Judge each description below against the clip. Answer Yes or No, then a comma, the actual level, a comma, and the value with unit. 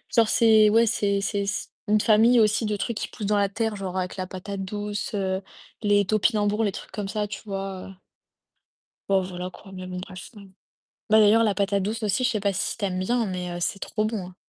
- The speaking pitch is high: Yes, high, 205 Hz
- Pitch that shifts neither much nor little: No, narrow, 2.1 semitones